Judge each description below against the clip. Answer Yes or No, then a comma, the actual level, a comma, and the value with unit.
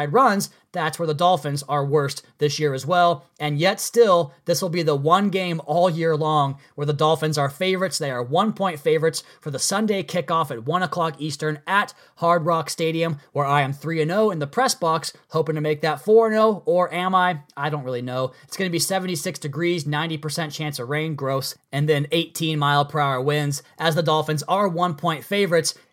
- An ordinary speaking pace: No, fast, 215 wpm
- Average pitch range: Yes, average, 3.1 semitones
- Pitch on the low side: No, medium, 160 Hz